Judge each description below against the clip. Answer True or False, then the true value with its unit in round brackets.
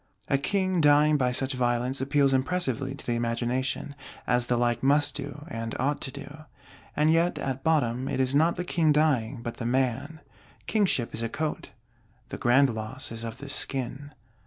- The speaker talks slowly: False (185 wpm)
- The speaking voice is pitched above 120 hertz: True (135 Hz)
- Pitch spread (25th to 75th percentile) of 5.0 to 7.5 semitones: False (3.4 semitones)